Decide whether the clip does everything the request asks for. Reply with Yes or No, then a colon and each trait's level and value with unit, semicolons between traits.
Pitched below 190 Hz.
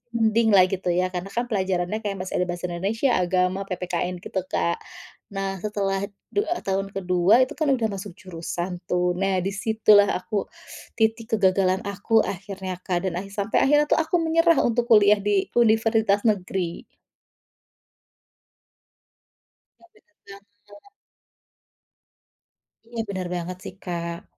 No: high, 195 Hz